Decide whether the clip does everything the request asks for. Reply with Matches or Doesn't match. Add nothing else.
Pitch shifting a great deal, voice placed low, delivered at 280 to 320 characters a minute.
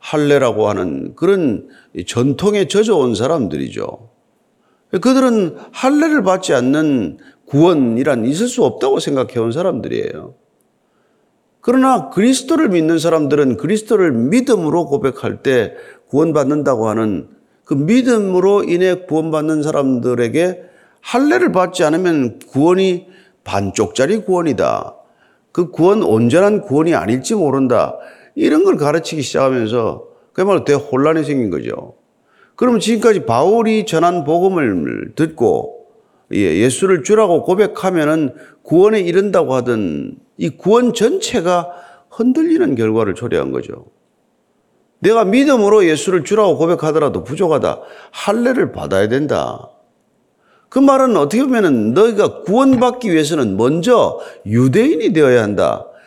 Doesn't match